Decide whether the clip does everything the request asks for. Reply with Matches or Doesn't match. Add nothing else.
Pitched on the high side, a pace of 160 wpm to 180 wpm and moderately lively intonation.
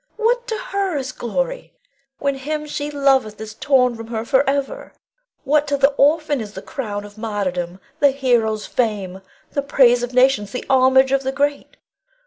Matches